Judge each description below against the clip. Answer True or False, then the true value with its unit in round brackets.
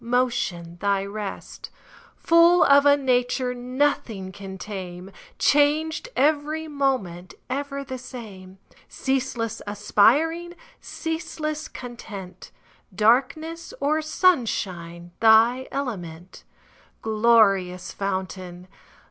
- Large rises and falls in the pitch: True (6.8 semitones)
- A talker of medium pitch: False (240 Hz)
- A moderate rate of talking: False (85 wpm)